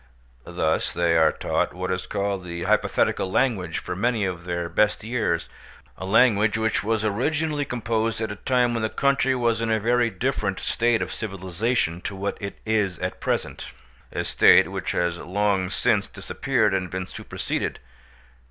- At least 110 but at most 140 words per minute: No, average, 165 wpm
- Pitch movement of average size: Yes, average, 4.1 semitones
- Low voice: Yes, low, 105 Hz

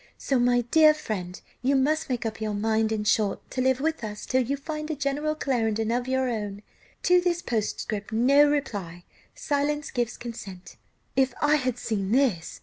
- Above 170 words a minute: Yes, average, 180 wpm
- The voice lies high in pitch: Yes, high, 245 Hz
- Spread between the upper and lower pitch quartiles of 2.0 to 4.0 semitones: No, average, 4.6 semitones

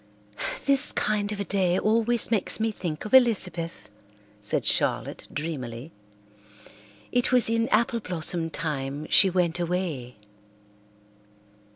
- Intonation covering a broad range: Yes, wide, 5.7 semitones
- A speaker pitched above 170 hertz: Yes, medium, 185 Hz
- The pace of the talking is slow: Yes, slow, 115 wpm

